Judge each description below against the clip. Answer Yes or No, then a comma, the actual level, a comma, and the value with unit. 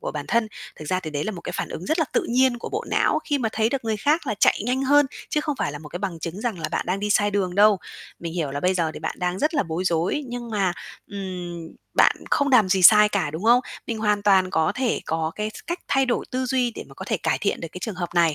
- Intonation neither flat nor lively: No, wide, 5.7 semitones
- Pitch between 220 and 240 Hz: No, high, 205 Hz